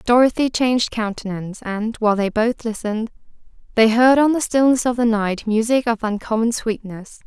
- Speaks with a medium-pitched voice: No, high, 225 Hz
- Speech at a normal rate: Yes, average, 165 wpm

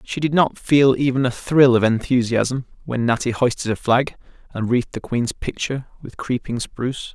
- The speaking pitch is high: No, low, 125 Hz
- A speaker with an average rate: Yes, average, 185 wpm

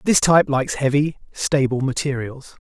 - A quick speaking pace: No, slow, 135 wpm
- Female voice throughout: No, male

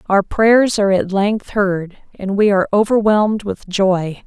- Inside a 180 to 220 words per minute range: No, average, 170 wpm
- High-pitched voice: Yes, high, 200 Hz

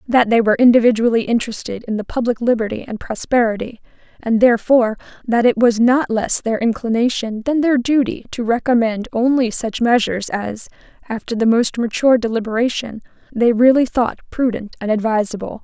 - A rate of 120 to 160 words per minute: Yes, average, 155 wpm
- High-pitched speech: Yes, high, 230 Hz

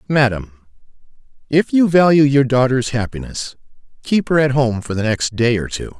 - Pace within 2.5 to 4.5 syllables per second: No, 5.0 syllables/s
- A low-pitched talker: Yes, low, 130 Hz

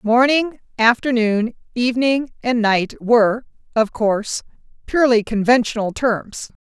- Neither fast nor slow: No, slow, 100 wpm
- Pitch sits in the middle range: No, high, 235 Hz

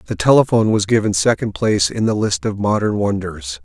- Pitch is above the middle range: No, low, 110 Hz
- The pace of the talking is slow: No, average, 200 wpm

